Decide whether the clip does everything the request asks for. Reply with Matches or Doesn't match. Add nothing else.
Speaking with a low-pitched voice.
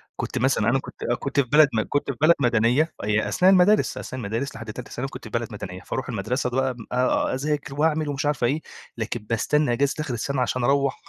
Matches